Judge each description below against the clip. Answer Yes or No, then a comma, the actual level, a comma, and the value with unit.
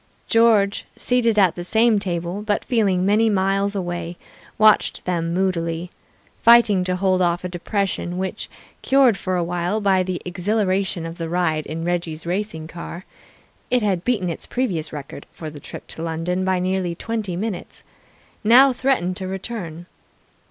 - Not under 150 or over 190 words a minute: Yes, average, 160 wpm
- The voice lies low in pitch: No, medium, 185 Hz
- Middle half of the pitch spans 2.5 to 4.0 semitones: Yes, average, 3.3 semitones